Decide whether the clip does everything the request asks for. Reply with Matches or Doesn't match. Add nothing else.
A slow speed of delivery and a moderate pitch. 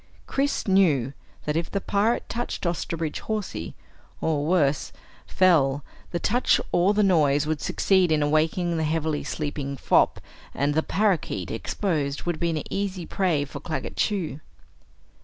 Doesn't match